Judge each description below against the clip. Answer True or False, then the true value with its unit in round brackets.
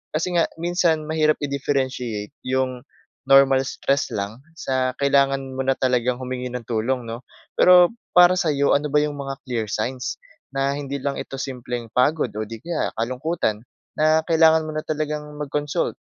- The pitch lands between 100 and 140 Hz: True (135 Hz)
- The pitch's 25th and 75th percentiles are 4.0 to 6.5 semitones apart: False (3.4 semitones)